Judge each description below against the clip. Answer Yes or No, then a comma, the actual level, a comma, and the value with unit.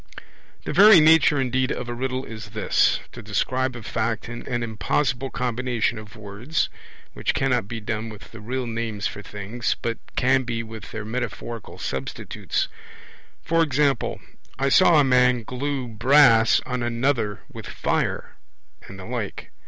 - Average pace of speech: Yes, average, 150 wpm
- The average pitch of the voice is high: No, low, 120 Hz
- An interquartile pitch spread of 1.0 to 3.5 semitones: Yes, average, 2.9 semitones